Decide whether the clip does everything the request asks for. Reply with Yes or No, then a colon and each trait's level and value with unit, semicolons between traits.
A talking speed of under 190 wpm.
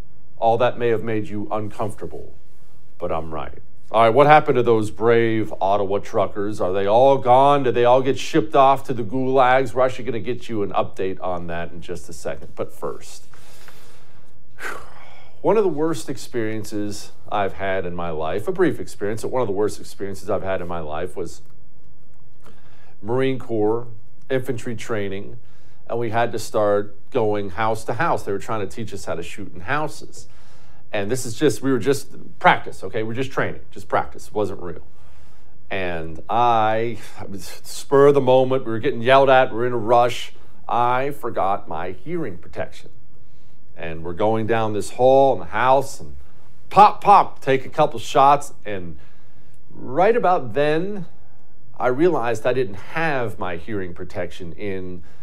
Yes: average, 180 wpm